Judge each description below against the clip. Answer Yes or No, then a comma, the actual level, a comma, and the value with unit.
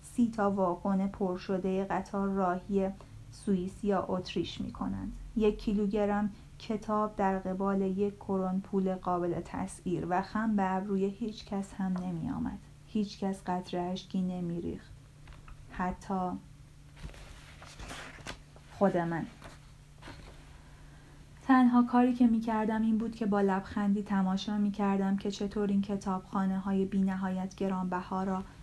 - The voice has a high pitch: Yes, high, 195 Hz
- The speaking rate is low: No, average, 125 wpm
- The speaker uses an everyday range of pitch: No, narrow, 1.8 semitones